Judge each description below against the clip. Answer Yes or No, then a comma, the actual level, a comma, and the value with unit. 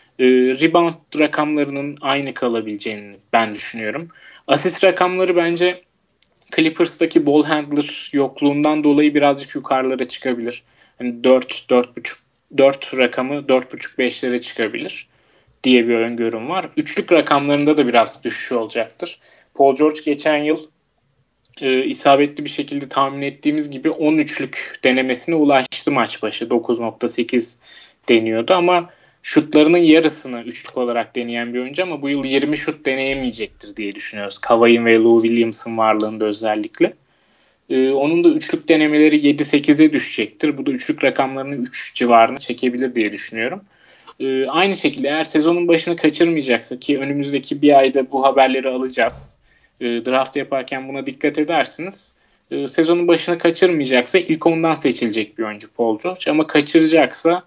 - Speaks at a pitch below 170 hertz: Yes, medium, 140 Hz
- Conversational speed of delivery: Yes, average, 130 wpm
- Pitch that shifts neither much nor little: Yes, average, 4.1 semitones